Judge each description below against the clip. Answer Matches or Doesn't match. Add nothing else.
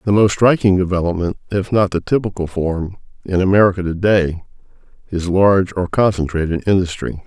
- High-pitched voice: Doesn't match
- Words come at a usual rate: Matches